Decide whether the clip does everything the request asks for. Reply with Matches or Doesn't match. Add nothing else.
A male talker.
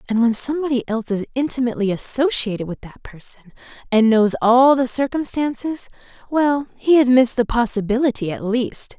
Doesn't match